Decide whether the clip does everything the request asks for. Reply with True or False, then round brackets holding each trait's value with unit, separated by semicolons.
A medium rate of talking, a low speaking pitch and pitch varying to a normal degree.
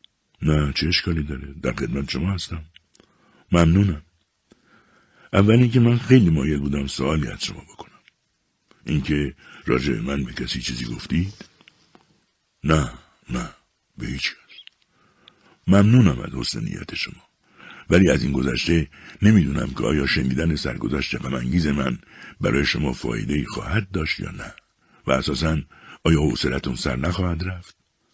True (130 wpm; 80 Hz; 4.4 semitones)